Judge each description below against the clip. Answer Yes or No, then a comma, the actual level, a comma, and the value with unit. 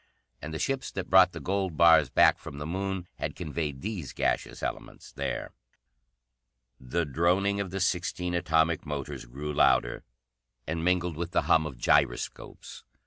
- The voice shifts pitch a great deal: No, average, 3.6 semitones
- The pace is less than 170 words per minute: Yes, average, 155 wpm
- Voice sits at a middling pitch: No, very low, 85 Hz